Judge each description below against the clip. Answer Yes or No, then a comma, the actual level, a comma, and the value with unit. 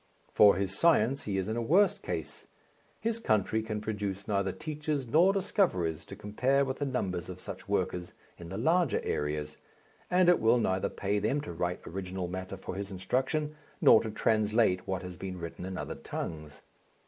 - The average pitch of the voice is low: Yes, low, 105 Hz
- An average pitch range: No, wide, 6.7 semitones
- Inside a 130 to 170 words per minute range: No, average, 185 wpm